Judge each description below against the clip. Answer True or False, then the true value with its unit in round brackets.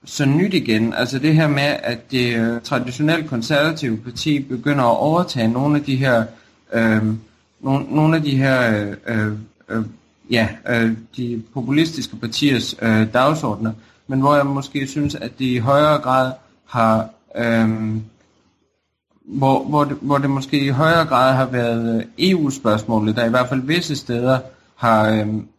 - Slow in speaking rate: False (155 wpm)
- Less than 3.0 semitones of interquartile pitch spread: False (4.1 semitones)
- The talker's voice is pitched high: False (125 Hz)